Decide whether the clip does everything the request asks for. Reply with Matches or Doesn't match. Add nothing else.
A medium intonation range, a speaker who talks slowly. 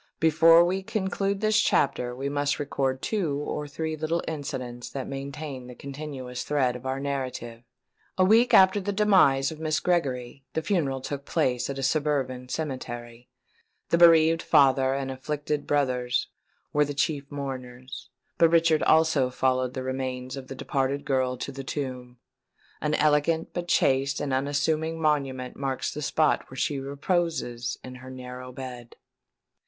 Doesn't match